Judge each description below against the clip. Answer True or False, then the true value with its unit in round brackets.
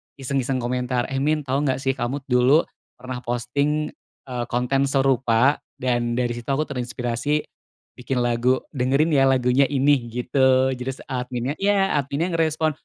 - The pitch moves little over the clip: True (2.3 semitones)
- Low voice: True (130 Hz)